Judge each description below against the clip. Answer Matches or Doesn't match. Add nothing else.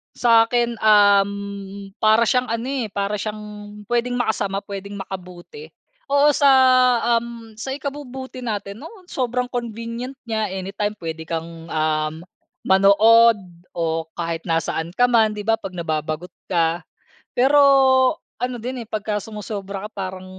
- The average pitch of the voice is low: Doesn't match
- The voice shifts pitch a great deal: Doesn't match